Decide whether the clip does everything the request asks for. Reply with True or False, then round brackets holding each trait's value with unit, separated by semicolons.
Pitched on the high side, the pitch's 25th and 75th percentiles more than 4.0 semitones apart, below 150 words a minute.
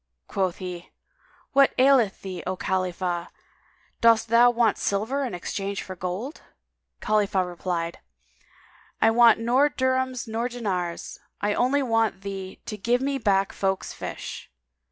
True (210 Hz; 4.5 semitones; 135 wpm)